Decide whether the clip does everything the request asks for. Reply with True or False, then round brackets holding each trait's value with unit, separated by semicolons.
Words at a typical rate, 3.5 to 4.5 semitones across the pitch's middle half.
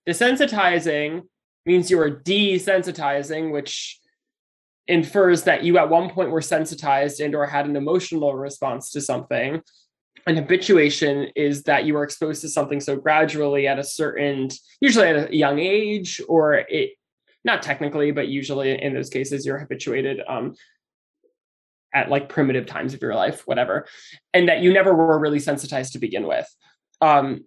True (155 wpm; 4.2 semitones)